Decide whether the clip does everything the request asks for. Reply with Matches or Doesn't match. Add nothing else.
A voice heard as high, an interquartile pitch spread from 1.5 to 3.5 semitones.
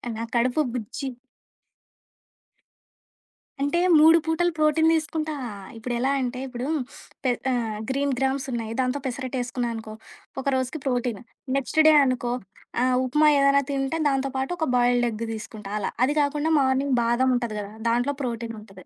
Matches